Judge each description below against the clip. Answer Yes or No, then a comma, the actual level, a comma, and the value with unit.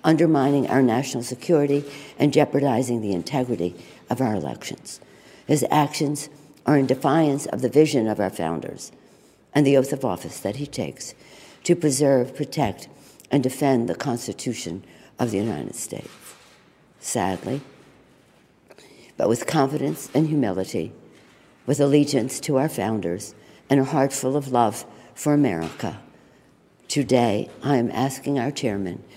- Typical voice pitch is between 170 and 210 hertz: No, low, 135 Hz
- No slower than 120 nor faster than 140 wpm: Yes, slow, 135 wpm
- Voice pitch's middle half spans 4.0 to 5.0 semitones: Yes, average, 4.7 semitones